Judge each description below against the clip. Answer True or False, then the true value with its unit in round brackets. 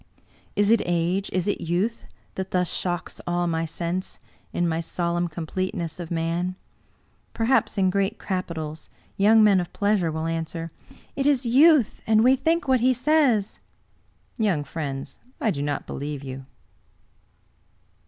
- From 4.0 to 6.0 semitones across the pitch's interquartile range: True (5.0 semitones)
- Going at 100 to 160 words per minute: True (155 wpm)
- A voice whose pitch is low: False (180 Hz)